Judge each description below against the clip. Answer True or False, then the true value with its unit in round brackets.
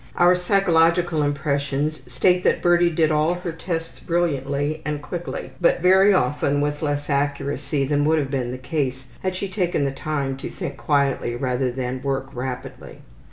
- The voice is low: False (145 Hz)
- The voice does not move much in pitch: False (3.8 semitones)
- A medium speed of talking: True (165 wpm)